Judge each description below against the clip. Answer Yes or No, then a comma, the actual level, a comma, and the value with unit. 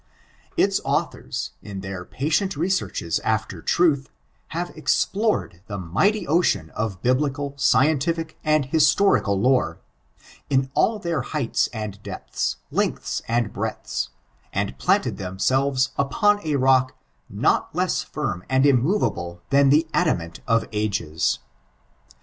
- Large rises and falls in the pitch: Yes, wide, 7.4 semitones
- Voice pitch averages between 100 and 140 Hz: Yes, low, 135 Hz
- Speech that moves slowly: Yes, slow, 120 wpm